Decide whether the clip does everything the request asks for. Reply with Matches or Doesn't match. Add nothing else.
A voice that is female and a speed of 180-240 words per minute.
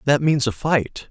Doesn't match